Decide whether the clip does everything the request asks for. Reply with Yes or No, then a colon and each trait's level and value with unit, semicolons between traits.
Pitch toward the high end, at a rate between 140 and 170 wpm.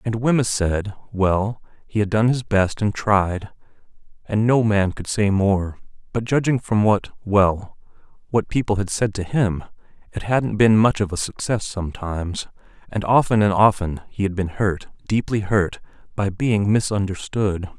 No: low, 105 Hz; average, 160 wpm